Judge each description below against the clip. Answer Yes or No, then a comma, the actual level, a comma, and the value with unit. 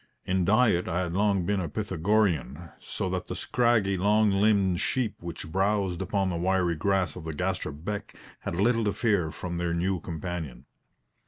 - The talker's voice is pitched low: Yes, very low, 95 Hz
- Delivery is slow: No, average, 175 wpm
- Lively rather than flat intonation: No, average, 3.2 semitones